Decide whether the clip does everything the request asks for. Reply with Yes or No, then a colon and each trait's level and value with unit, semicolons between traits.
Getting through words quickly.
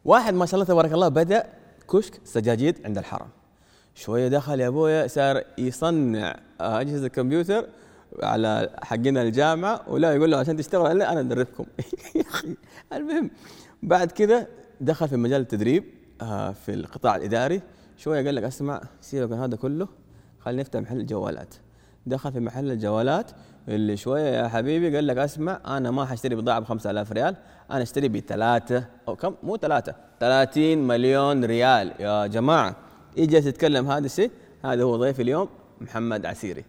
Yes: fast, 155 wpm